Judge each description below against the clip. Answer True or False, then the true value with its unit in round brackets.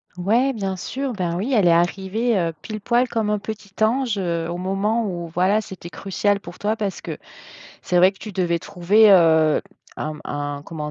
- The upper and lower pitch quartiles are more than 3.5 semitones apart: True (3.9 semitones)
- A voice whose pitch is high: True (195 Hz)